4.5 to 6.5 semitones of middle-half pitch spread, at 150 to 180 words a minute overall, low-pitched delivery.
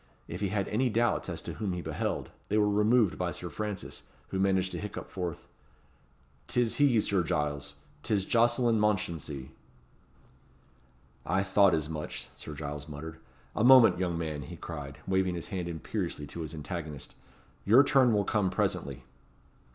Yes: average, 5.1 semitones; average, 160 wpm; very low, 95 Hz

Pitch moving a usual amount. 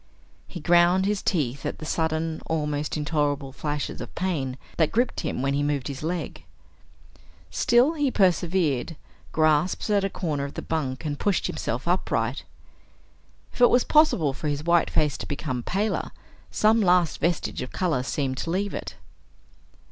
Yes: average, 4.4 semitones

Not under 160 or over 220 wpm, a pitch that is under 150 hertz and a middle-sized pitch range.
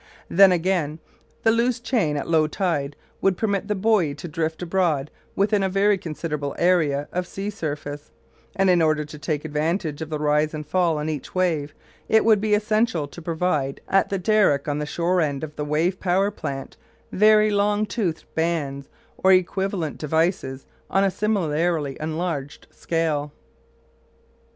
No: average, 165 wpm; medium, 165 Hz; average, 4.5 semitones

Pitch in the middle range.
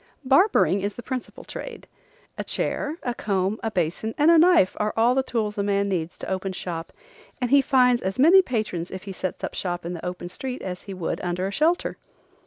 No: high, 210 Hz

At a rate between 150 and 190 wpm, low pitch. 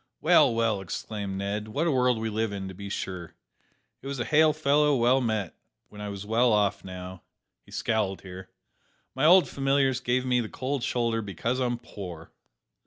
Yes: average, 180 wpm; low, 115 Hz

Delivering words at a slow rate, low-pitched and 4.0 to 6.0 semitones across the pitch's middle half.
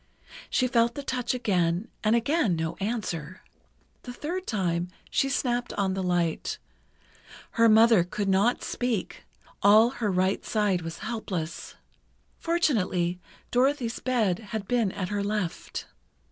No: slow, 130 wpm; high, 210 Hz; average, 4.9 semitones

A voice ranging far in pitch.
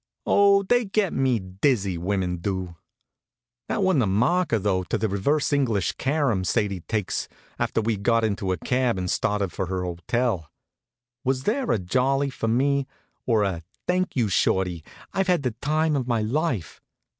Yes: wide, 6.8 semitones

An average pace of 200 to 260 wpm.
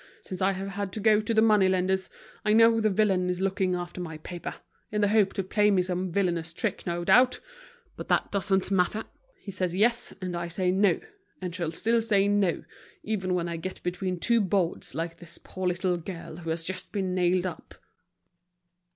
Yes: fast, 205 wpm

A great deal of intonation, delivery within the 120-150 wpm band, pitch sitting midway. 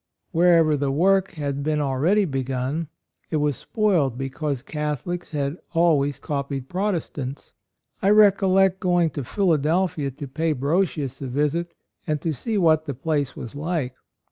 No: average, 4.1 semitones; average, 140 wpm; medium, 150 Hz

